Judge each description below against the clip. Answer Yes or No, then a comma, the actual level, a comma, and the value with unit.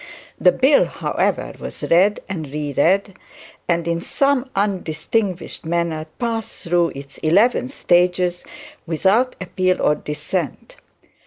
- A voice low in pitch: No, medium, 180 Hz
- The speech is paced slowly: Yes, slow, 110 wpm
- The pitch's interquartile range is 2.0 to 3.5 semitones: No, average, 4.1 semitones